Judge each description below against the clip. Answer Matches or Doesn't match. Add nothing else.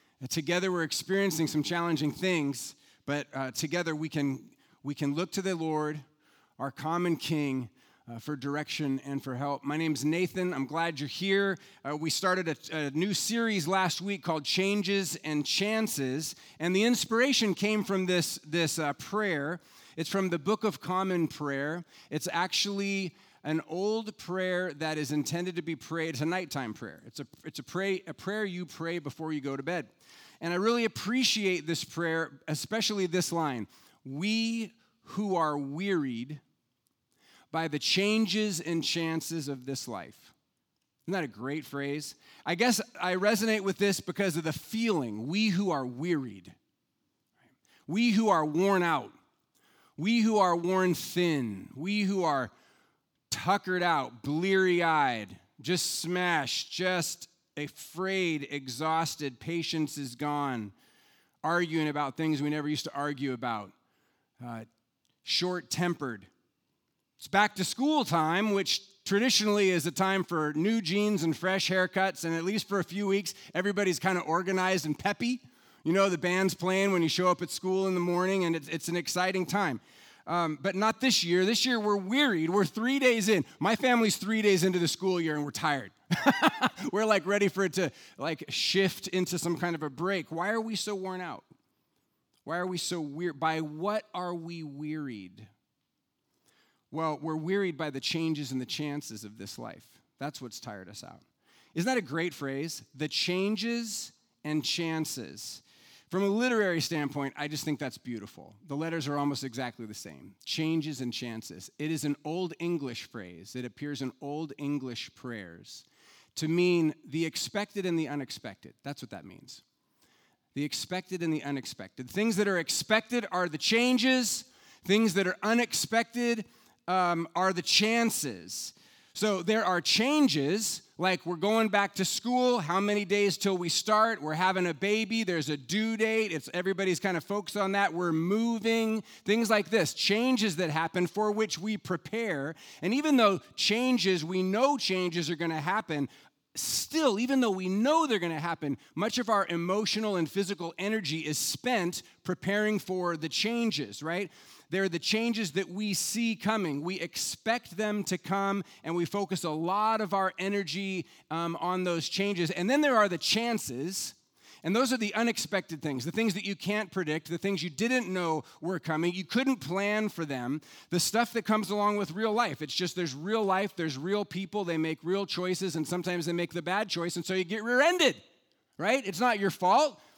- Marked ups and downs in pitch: Doesn't match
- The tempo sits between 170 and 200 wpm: Matches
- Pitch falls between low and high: Matches